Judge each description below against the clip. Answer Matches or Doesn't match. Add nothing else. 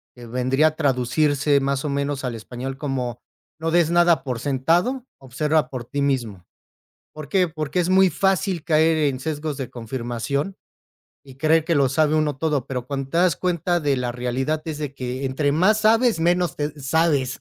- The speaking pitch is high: Doesn't match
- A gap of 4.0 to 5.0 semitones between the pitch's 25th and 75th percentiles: Doesn't match